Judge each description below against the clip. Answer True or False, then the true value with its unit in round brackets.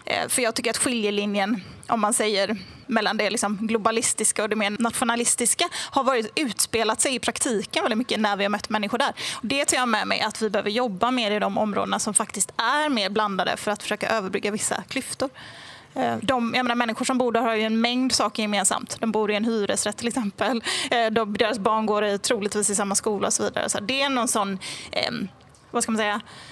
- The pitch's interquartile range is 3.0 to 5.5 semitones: False (2.5 semitones)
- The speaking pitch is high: True (220 Hz)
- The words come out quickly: True (220 wpm)